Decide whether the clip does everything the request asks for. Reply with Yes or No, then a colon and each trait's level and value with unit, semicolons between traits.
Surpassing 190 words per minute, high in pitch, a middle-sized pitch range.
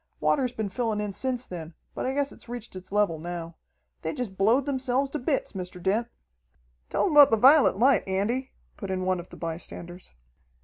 No: average, 200 wpm; high, 215 Hz; wide, 5.8 semitones